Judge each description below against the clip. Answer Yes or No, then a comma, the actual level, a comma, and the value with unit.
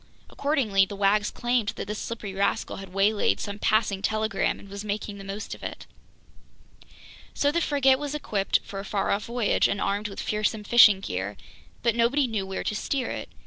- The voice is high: Yes, high, 210 Hz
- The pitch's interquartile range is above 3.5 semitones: No, average, 3.0 semitones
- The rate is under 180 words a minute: No, average, 190 wpm